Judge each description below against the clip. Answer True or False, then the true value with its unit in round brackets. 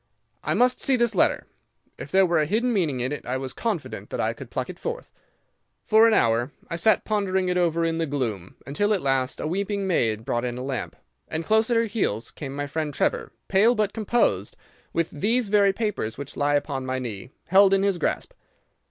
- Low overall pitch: False (170 Hz)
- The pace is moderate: False (215 wpm)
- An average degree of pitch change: False (7.7 semitones)